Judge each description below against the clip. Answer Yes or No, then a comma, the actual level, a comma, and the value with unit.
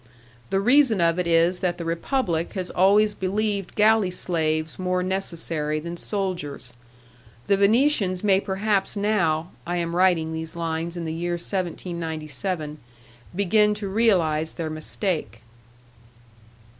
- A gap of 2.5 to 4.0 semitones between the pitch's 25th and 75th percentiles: Yes, average, 3.4 semitones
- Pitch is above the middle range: No, medium, 180 Hz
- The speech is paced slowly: Yes, slow, 130 wpm